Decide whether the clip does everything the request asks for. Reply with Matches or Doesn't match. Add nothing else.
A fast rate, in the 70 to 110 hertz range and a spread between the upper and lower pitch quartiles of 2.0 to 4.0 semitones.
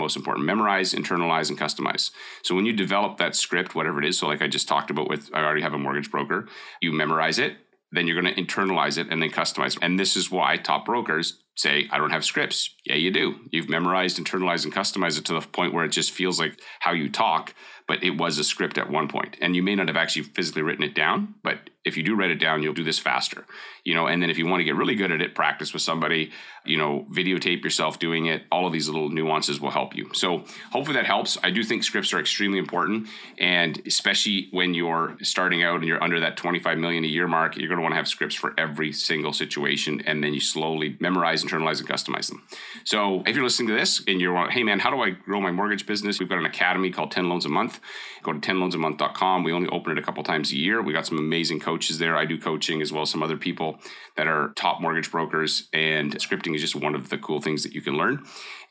Matches